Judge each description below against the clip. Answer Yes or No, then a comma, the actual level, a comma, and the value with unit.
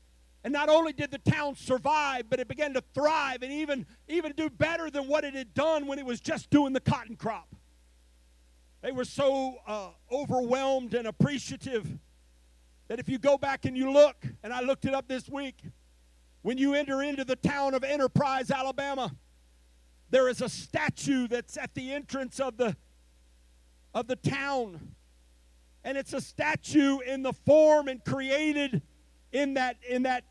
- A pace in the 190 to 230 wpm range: No, average, 170 wpm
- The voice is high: Yes, very high, 260 Hz